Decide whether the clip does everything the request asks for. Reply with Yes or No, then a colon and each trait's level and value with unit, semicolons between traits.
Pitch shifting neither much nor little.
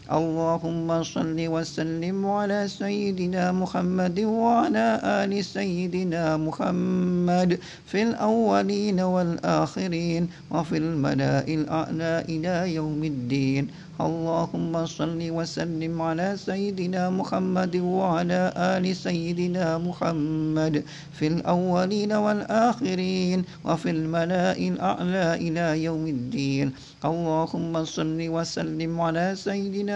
No: narrow, 2.3 semitones